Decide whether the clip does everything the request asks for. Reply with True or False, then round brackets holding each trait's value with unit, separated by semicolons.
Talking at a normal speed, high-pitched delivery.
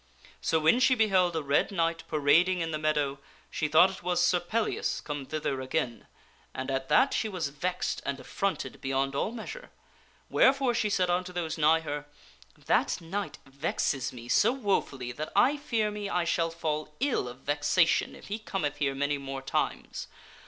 False (180 wpm; 165 Hz)